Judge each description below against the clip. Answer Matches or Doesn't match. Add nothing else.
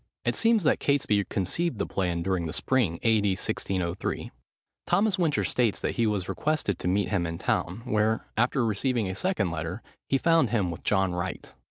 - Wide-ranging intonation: Matches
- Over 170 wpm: Matches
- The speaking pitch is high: Doesn't match